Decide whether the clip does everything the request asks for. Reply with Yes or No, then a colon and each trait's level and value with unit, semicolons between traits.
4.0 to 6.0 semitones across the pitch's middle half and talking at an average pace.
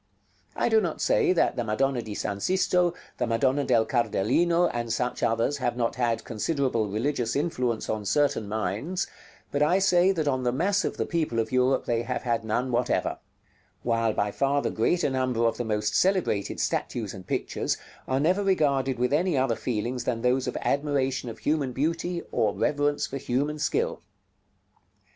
Yes: average, 4.6 semitones; average, 180 wpm